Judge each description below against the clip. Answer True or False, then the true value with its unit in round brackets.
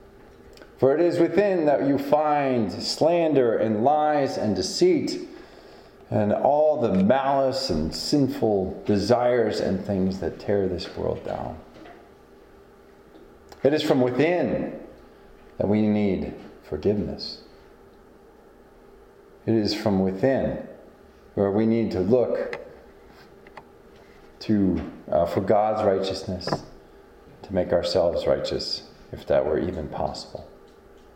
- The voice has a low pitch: True (125 Hz)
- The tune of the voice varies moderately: False (6.9 semitones)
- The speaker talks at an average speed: False (110 wpm)